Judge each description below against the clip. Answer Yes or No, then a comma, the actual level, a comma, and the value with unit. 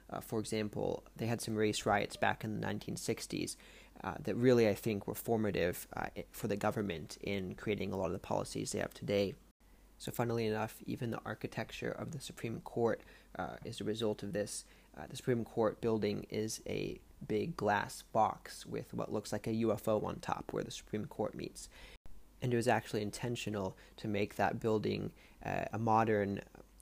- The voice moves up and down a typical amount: No, narrow, 1.7 semitones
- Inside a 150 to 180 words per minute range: No, average, 190 wpm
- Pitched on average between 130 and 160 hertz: No, low, 110 Hz